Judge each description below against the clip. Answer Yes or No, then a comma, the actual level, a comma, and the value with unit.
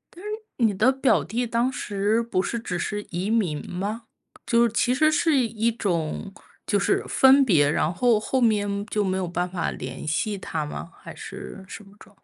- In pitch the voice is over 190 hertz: Yes, high, 210 Hz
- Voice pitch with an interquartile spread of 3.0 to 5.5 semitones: Yes, average, 4.2 semitones